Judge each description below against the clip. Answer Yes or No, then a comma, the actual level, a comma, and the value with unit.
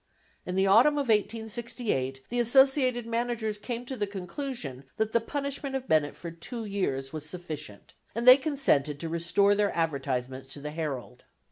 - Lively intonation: Yes, wide, 8.1 semitones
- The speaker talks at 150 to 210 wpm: Yes, average, 165 wpm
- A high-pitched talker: Yes, high, 205 Hz